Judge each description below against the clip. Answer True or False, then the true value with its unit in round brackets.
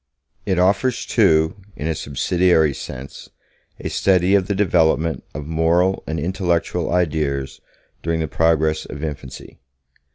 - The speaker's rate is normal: False (130 wpm)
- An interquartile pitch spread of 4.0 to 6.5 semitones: False (2.7 semitones)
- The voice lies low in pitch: True (80 Hz)